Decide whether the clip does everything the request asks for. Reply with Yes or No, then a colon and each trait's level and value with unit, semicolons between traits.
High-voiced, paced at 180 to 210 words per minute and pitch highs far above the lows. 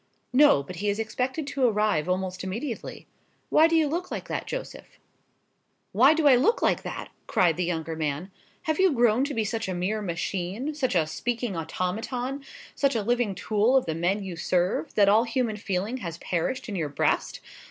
Yes: high, 215 Hz; average, 195 wpm; wide, 6.1 semitones